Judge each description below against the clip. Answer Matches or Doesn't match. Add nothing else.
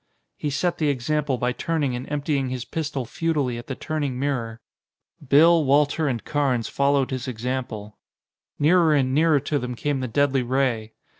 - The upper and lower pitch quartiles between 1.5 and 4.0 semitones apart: Matches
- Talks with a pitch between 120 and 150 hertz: Matches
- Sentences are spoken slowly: Doesn't match